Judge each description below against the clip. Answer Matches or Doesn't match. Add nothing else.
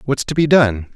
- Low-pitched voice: Matches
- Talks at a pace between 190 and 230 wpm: Doesn't match